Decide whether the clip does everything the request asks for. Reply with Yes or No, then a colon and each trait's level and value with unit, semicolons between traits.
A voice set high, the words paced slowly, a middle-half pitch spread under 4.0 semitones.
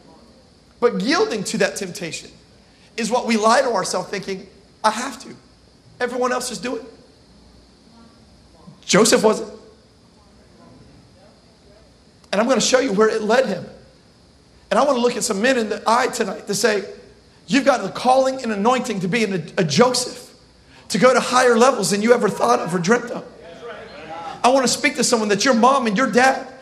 No: high, 235 Hz; average, 185 wpm; average, 2.9 semitones